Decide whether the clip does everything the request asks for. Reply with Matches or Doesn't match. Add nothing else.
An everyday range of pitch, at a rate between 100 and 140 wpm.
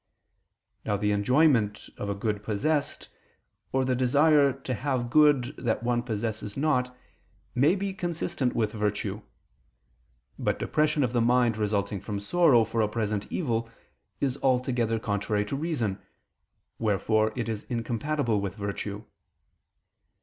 Matches